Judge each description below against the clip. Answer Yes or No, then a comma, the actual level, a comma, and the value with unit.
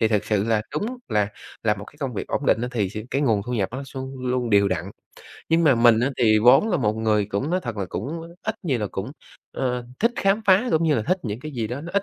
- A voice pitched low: Yes, low, 125 Hz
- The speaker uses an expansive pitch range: Yes, wide, 6.2 semitones